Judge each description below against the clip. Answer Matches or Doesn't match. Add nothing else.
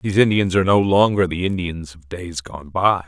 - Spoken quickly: Matches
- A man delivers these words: Matches